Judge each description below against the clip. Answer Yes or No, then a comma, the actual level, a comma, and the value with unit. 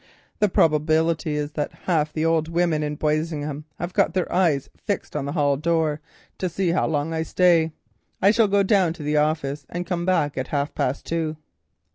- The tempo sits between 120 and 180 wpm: No, average, 195 wpm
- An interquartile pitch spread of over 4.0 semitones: No, average, 2.7 semitones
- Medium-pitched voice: Yes, medium, 160 Hz